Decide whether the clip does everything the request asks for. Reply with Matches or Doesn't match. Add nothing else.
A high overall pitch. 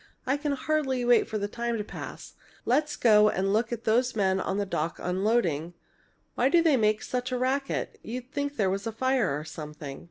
Matches